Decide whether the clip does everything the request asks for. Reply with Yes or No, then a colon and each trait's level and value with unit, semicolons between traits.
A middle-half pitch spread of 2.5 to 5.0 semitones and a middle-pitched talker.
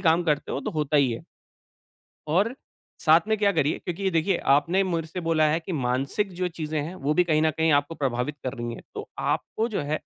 Yes: average, 3.5 semitones; medium, 160 Hz